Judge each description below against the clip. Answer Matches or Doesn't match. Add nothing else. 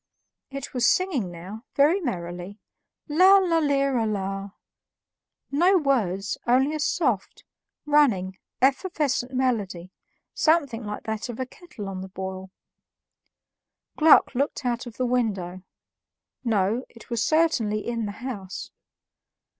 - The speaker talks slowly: Matches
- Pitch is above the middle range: Matches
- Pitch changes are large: Matches